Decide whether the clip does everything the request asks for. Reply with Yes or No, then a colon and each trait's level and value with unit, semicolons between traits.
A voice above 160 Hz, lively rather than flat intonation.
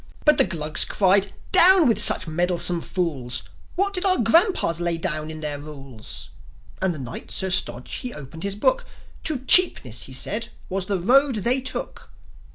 Yes: medium, 185 Hz; wide, 8.8 semitones